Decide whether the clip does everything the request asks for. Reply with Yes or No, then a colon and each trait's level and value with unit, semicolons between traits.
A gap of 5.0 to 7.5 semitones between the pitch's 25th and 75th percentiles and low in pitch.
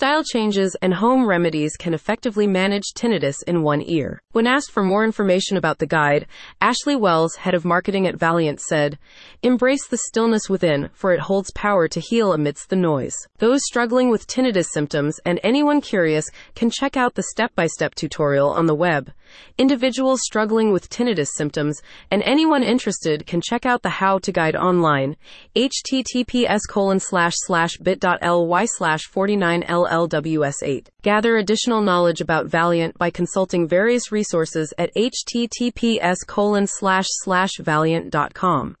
No: wide, 5.4 semitones; high, 190 Hz